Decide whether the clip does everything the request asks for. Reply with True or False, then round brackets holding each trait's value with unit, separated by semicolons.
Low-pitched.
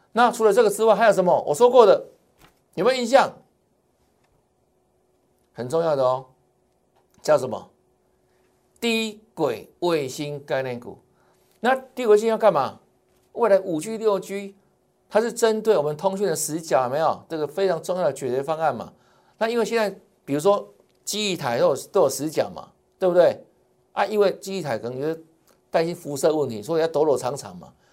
False (195 Hz)